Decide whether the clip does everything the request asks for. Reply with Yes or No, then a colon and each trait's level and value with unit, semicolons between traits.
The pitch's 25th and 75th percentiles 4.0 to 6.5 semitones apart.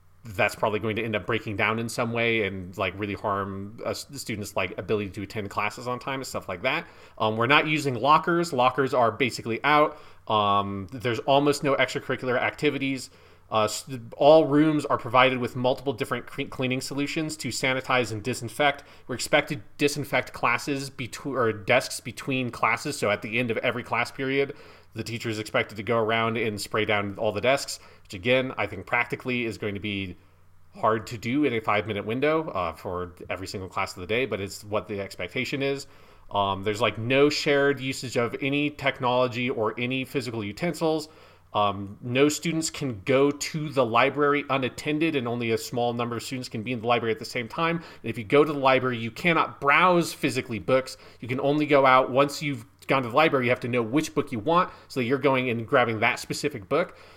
Yes: average, 4.3 semitones